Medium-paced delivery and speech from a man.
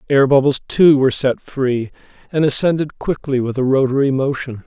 Yes: average, 165 wpm; male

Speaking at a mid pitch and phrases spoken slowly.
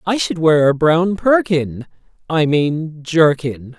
Yes: medium, 160 Hz; slow, 125 wpm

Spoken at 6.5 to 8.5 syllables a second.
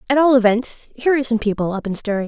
Yes: 7.2 syllables/s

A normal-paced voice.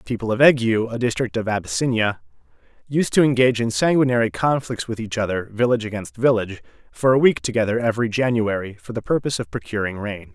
Yes: average, 185 wpm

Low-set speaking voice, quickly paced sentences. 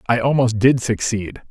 No: low, 115 Hz; average, 160 wpm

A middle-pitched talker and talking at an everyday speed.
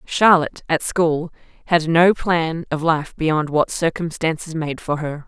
Yes: medium, 160 Hz; average, 160 wpm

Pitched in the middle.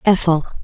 Yes: medium, 175 Hz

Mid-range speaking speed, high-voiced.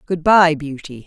No: average, 170 wpm; medium, 160 Hz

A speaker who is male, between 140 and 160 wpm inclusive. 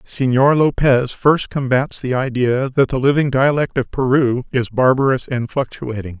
Yes: male; average, 155 wpm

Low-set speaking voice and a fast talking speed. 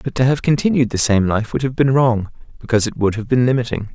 Yes: low, 120 Hz; fast, 260 wpm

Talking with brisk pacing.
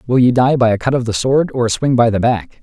Yes: fast, 345 wpm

